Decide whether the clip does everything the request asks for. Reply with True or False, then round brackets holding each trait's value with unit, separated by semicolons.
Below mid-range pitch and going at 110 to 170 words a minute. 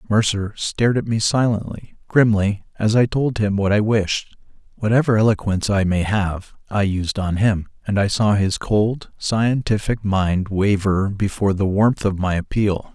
True (105 Hz; 165 wpm)